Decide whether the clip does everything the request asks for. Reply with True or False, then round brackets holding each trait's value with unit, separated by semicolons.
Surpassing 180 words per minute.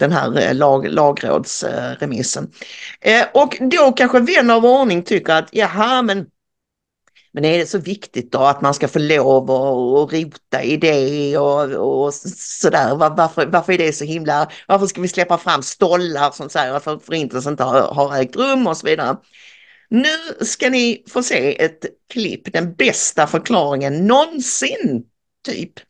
False (165 wpm)